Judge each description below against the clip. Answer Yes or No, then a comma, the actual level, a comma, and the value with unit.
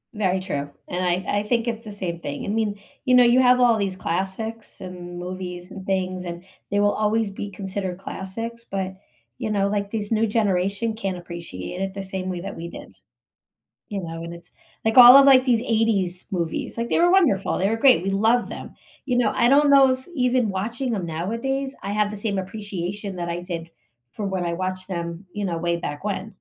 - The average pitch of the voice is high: Yes, high, 200 Hz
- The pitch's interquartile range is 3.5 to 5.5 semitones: Yes, average, 3.8 semitones